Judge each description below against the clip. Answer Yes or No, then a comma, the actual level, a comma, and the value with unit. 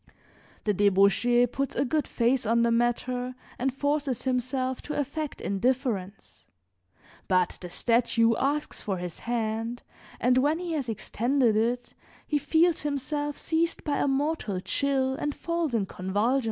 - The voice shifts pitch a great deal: No, average, 4.0 semitones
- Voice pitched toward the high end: Yes, very high, 250 Hz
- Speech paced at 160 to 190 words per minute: No, average, 145 wpm